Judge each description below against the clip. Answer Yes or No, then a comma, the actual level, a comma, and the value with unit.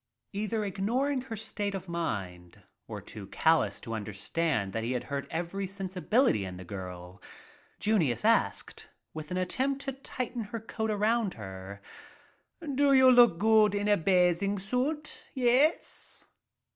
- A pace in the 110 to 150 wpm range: Yes, average, 140 wpm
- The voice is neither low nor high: No, high, 195 Hz